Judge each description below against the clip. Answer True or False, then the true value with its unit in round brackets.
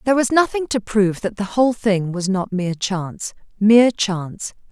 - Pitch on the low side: False (210 Hz)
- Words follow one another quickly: False (190 wpm)